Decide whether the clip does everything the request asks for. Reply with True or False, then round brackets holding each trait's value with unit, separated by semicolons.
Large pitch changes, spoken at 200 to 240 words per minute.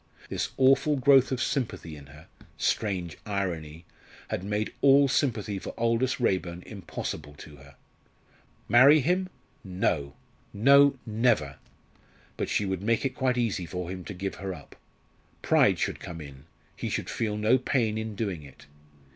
False (6.6 semitones; 155 wpm)